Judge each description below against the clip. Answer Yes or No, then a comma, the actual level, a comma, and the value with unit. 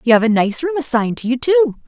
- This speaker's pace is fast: Yes, fast, 285 wpm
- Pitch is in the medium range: No, very high, 265 Hz